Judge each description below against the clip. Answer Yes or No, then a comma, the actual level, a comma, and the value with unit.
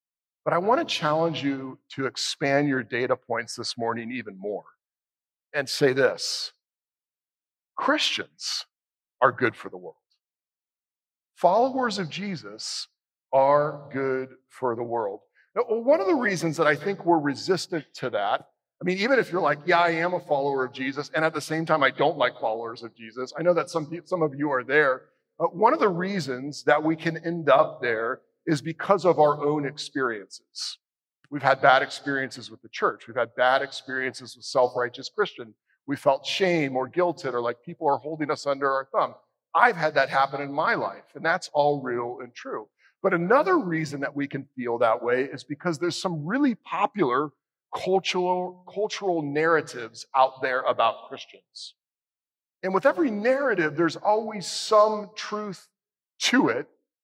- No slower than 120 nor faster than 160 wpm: No, average, 175 wpm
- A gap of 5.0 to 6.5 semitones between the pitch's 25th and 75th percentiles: Yes, wide, 5.5 semitones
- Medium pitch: Yes, medium, 155 Hz